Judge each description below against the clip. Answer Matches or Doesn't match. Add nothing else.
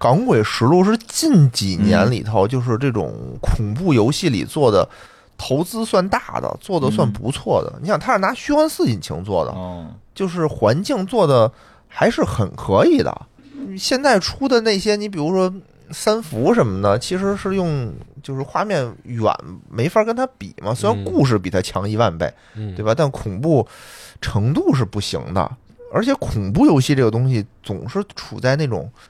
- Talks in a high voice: Doesn't match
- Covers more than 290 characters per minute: Doesn't match